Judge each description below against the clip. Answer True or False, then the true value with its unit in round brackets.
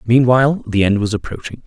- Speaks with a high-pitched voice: False (115 Hz)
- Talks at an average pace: True (180 wpm)